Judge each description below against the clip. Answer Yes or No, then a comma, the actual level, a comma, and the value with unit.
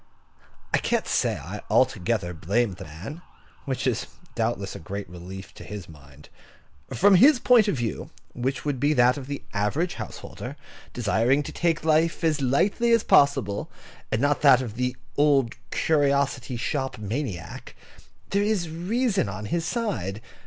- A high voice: No, low, 135 Hz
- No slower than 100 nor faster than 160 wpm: Yes, average, 155 wpm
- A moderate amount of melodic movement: No, wide, 7.5 semitones